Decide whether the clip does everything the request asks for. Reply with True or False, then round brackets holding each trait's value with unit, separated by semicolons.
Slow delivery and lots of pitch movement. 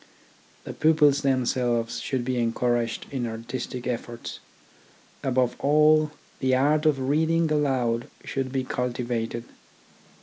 False (115 wpm; 3.3 semitones)